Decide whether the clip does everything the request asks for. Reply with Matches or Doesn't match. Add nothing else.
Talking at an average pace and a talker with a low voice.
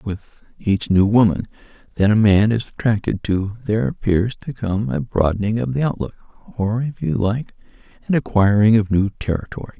Matches